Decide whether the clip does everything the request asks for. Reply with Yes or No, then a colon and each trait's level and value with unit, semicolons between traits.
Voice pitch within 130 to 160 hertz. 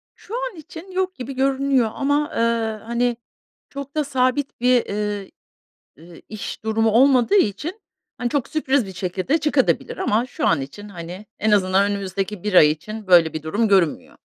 No: high, 225 Hz